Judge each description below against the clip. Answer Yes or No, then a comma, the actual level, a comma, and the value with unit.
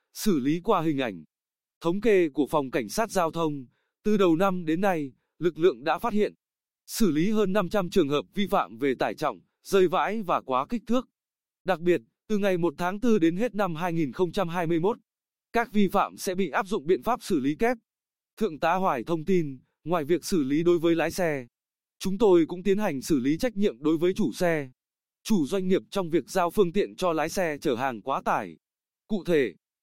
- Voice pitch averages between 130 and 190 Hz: Yes, medium, 185 Hz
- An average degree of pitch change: Yes, average, 4.1 semitones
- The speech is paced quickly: No, average, 215 wpm